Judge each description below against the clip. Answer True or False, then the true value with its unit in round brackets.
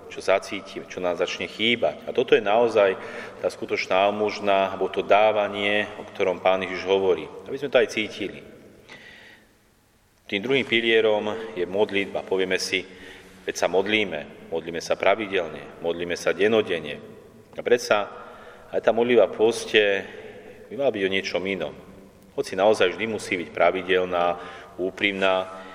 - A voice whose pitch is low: True (100 Hz)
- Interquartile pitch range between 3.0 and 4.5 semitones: True (3.6 semitones)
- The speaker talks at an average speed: True (140 wpm)